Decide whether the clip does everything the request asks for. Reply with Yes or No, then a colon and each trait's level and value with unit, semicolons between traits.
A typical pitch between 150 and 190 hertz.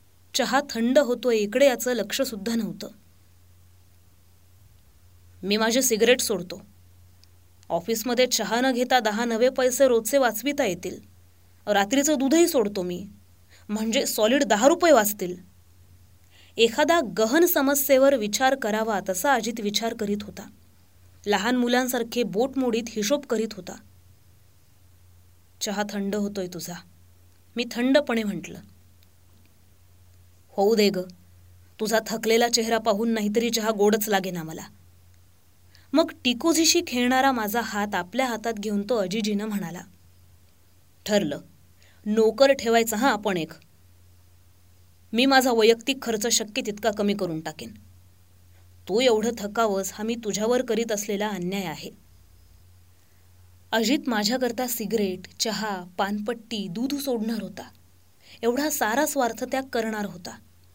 No: high, 210 Hz